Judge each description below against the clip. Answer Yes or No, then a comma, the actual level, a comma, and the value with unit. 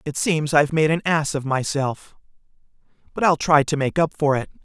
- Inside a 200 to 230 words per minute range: Yes, fast, 205 wpm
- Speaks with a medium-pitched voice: Yes, medium, 150 Hz